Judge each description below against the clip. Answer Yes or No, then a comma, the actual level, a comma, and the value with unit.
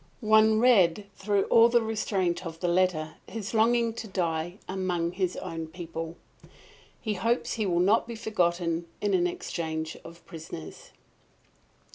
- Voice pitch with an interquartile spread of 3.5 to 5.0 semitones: Yes, average, 4.4 semitones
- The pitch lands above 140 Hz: Yes, medium, 185 Hz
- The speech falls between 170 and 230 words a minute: No, average, 145 wpm